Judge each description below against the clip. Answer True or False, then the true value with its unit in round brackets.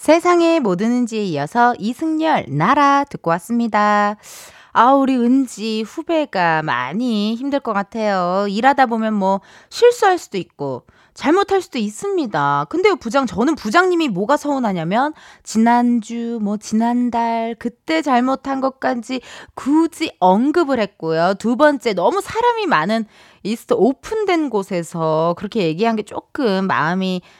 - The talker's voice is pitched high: True (235 Hz)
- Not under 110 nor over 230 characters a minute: False (285 characters per minute)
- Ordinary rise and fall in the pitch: False (6.1 semitones)